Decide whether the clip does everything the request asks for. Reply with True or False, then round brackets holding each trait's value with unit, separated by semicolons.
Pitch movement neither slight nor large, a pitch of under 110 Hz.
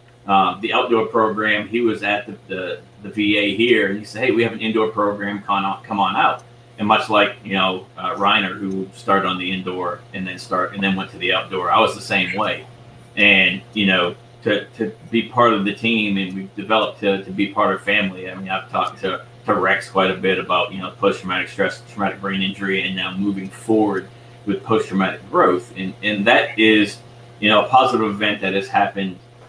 False (2.2 semitones; 100 Hz)